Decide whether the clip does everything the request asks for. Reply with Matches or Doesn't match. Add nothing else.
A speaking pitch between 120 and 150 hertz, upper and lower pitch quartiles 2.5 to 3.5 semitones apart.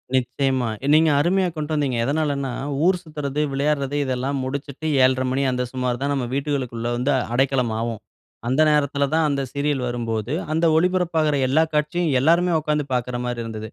Matches